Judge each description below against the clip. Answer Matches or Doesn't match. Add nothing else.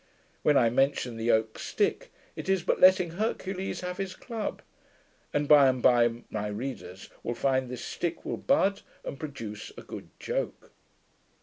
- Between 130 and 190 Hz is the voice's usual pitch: Matches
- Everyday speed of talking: Matches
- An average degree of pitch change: Doesn't match